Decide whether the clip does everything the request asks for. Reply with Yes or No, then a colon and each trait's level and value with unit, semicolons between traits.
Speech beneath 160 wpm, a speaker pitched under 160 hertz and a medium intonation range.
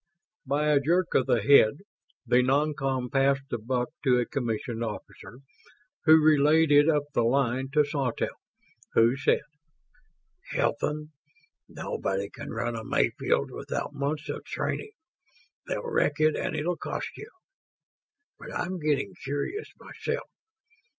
Yes: slow, 135 wpm; medium, 140 Hz; average, 3.8 semitones